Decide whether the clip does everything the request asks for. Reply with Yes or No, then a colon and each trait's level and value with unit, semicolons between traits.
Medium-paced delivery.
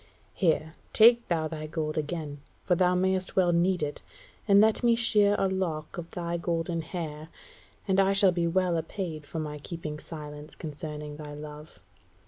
Yes: average, 170 wpm